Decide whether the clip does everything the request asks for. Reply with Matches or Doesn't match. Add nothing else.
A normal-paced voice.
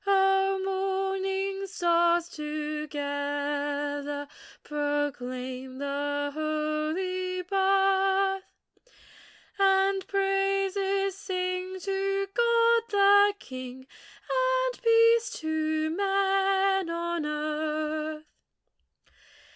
Doesn't match